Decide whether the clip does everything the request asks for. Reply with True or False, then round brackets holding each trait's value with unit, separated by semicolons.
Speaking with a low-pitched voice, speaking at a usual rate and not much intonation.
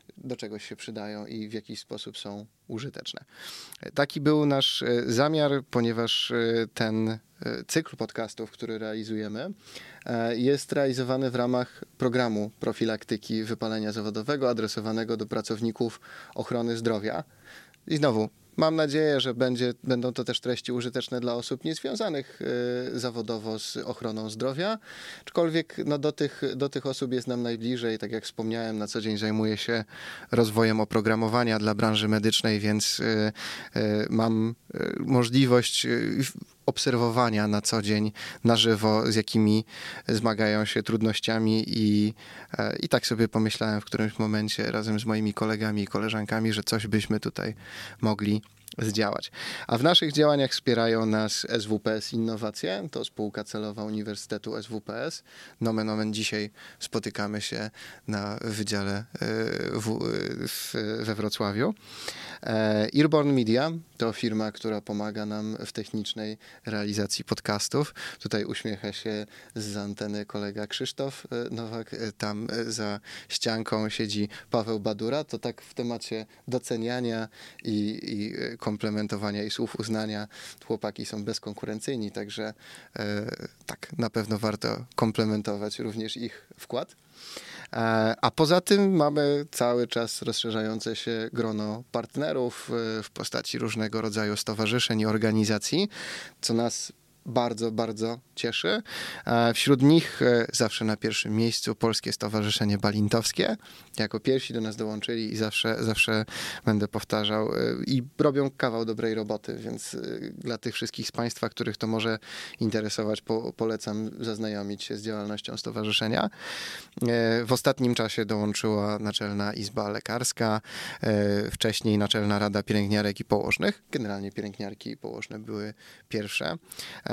True (110 Hz; 125 wpm; 1.8 semitones)